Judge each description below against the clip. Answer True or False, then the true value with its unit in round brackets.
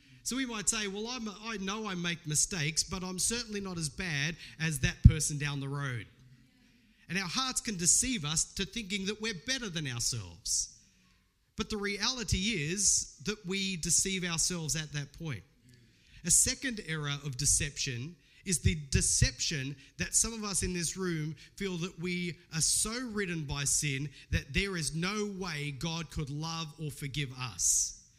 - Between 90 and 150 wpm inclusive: False (170 wpm)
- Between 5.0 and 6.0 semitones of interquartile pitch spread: True (5.6 semitones)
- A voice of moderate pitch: True (165 Hz)